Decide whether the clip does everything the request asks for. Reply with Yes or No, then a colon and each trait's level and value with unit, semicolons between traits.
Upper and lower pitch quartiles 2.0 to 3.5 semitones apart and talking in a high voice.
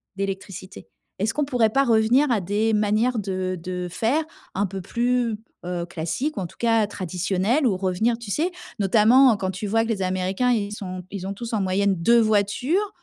No: average, 3.9 semitones; high, 205 Hz